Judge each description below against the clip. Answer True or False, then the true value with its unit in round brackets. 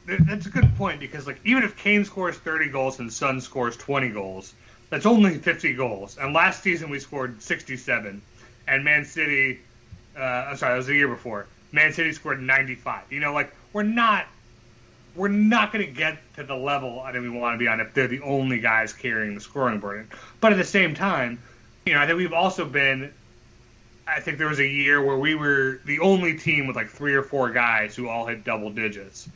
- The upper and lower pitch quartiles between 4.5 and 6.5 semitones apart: True (4.8 semitones)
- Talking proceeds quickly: True (215 wpm)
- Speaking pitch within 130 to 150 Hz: True (135 Hz)